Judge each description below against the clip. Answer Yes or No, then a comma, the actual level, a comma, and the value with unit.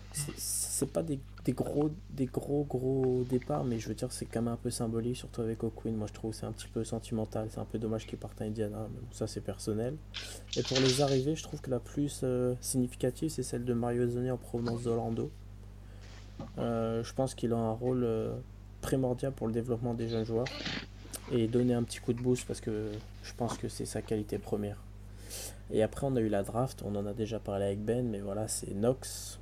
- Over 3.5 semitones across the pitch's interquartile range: No, average, 3.2 semitones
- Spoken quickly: Yes, fast, 230 wpm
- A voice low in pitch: Yes, low, 115 Hz